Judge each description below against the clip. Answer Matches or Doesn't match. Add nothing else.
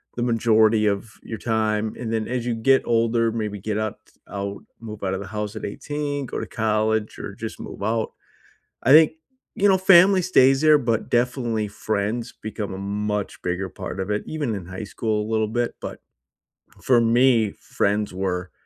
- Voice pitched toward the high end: Doesn't match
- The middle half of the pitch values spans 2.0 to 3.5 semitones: Matches